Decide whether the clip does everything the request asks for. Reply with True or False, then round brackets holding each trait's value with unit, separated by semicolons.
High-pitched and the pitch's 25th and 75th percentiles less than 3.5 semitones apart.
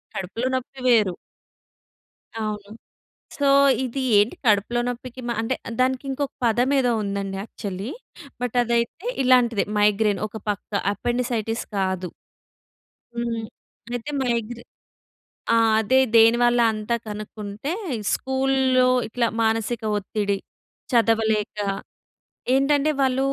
True (235 Hz; 3.1 semitones)